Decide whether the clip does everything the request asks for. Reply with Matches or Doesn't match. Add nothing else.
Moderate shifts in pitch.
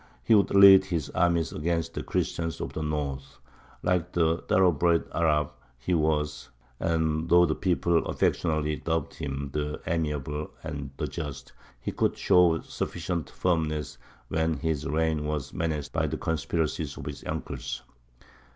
Doesn't match